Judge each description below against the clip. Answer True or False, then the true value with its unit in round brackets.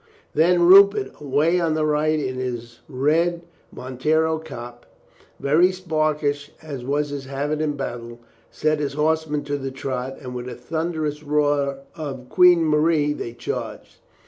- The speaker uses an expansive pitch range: False (2.8 semitones)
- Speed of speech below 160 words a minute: True (150 wpm)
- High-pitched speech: False (150 Hz)